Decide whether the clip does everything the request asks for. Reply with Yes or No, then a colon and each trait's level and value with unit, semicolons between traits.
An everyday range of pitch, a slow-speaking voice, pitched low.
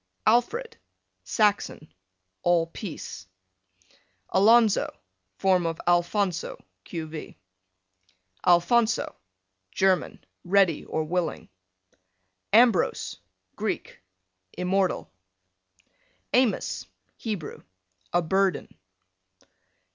No: average, 3.8 semitones; slow, 65 wpm; high, 190 Hz